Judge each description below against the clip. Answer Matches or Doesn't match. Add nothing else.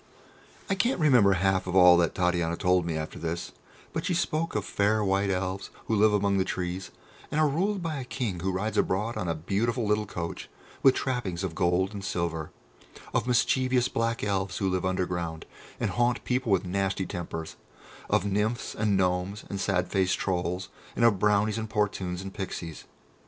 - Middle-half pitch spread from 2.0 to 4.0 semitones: Matches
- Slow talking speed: Doesn't match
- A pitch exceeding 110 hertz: Doesn't match